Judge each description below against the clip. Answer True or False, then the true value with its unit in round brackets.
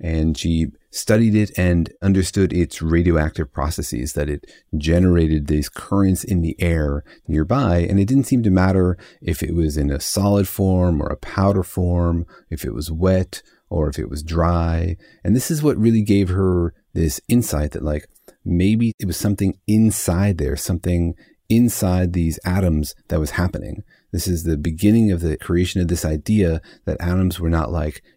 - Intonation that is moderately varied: True (3.4 semitones)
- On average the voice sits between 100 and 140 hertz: False (85 Hz)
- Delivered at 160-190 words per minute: True (175 wpm)